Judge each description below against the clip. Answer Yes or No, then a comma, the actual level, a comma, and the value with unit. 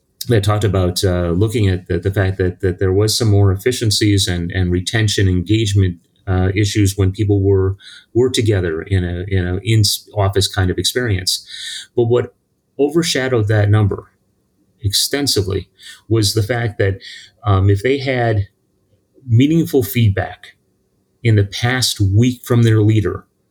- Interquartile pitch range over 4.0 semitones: No, average, 3.1 semitones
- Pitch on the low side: Yes, low, 100 Hz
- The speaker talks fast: No, average, 150 wpm